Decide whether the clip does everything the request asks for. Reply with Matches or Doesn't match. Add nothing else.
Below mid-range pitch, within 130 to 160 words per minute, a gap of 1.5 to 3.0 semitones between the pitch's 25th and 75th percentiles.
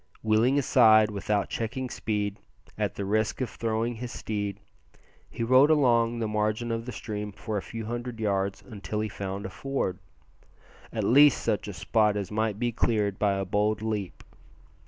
Doesn't match